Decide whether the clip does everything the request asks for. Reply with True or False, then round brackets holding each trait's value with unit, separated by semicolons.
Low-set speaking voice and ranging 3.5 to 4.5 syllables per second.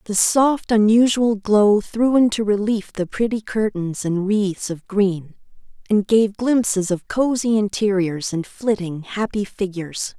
False (205 Hz; 4.0 syllables/s)